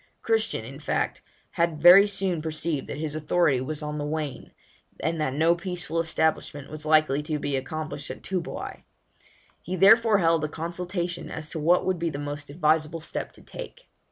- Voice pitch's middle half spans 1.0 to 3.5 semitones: Yes, average, 2.7 semitones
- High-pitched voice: No, medium, 160 Hz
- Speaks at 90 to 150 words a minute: No, average, 180 wpm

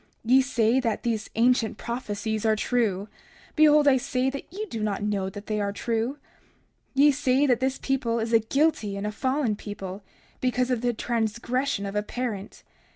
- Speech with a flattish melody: No, average, 3.6 semitones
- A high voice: Yes, high, 235 Hz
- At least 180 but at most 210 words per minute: Yes, average, 185 wpm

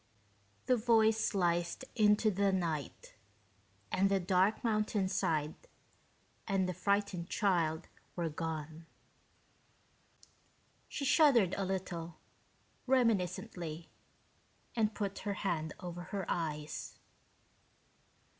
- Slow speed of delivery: Yes, slow, 90 wpm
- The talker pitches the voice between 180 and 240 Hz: Yes, high, 190 Hz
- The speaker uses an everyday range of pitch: Yes, average, 3.8 semitones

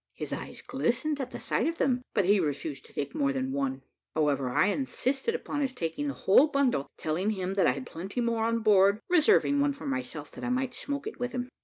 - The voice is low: No, high, 230 Hz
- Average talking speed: No, fast, 230 wpm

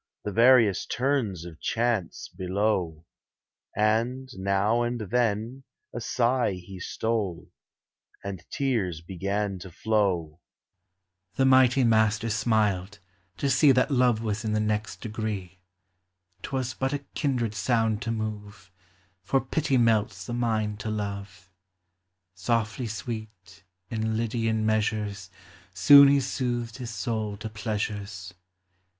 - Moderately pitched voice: No, low, 110 Hz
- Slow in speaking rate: Yes, slow, 125 wpm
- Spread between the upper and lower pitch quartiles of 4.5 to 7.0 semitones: No, average, 3.2 semitones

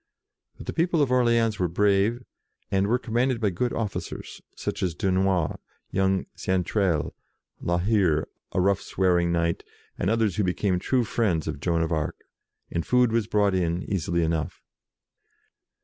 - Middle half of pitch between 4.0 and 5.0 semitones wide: Yes, average, 4.5 semitones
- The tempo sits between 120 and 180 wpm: Yes, average, 155 wpm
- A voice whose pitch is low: Yes, very low, 95 Hz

